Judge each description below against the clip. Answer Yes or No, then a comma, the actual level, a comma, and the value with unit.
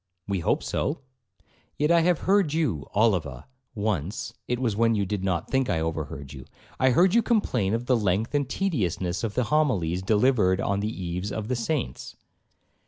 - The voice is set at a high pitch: No, low, 110 Hz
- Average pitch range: No, wide, 6.4 semitones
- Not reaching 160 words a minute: No, average, 180 wpm